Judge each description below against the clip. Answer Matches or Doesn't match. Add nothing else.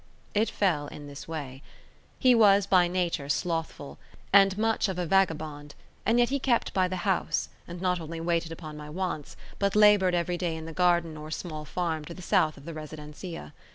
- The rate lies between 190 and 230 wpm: Matches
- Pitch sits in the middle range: Matches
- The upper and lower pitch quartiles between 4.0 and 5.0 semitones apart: Doesn't match